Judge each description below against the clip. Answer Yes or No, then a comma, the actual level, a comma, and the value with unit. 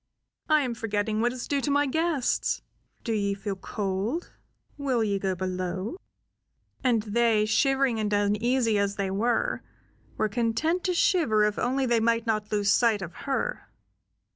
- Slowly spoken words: No, average, 160 wpm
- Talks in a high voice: Yes, high, 225 Hz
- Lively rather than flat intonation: No, average, 4.4 semitones